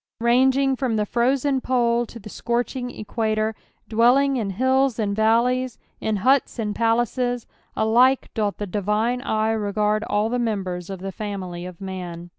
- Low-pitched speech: No, high, 225 Hz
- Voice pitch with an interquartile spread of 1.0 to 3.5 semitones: Yes, average, 3.1 semitones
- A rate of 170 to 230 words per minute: No, average, 155 wpm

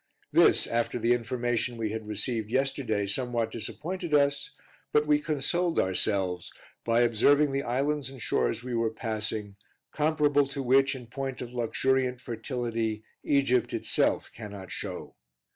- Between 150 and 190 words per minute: No, average, 140 wpm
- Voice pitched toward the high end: No, low, 120 Hz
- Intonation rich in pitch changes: No, average, 3.6 semitones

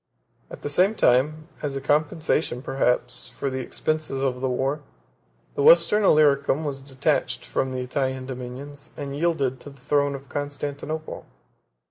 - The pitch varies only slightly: Yes, narrow, 2.3 semitones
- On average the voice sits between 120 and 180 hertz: Yes, medium, 140 Hz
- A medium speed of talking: Yes, average, 150 wpm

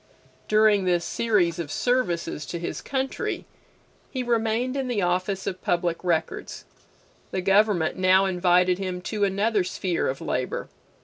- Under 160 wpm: Yes, average, 140 wpm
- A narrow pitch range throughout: No, average, 3.7 semitones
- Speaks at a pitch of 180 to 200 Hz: Yes, high, 190 Hz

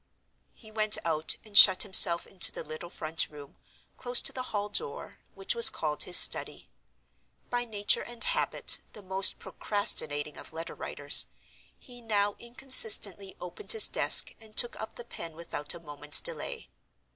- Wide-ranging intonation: Yes, wide, 6.1 semitones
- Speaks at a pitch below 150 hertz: No, high, 205 Hz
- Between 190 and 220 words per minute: No, average, 160 wpm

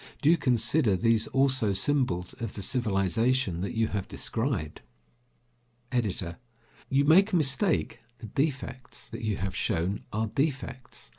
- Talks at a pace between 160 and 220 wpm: No, average, 140 wpm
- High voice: No, low, 115 Hz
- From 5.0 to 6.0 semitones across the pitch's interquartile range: Yes, average, 5.3 semitones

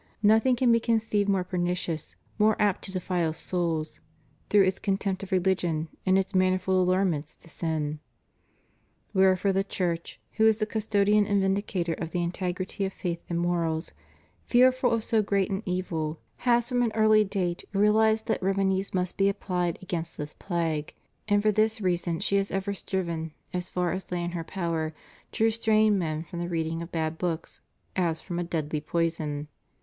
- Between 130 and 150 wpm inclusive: No, average, 175 wpm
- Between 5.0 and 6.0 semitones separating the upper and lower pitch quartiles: No, average, 3.3 semitones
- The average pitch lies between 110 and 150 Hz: No, medium, 185 Hz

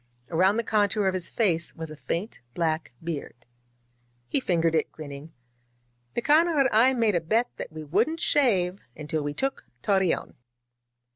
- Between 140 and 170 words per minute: Yes, average, 155 wpm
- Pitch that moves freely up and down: Yes, wide, 6.2 semitones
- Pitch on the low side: No, medium, 185 Hz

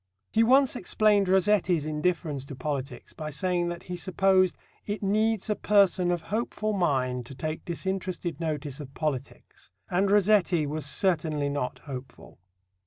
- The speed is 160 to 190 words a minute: No, average, 145 wpm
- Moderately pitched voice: Yes, medium, 175 Hz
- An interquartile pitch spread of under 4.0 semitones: No, average, 4.8 semitones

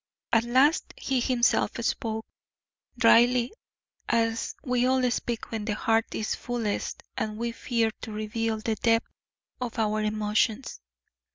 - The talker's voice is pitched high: Yes, high, 230 Hz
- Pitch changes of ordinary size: No, narrow, 1.7 semitones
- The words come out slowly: Yes, slow, 130 wpm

